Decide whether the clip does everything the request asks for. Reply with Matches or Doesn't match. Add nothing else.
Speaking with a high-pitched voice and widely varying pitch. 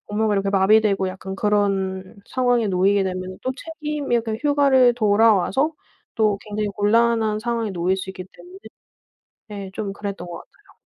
Doesn't match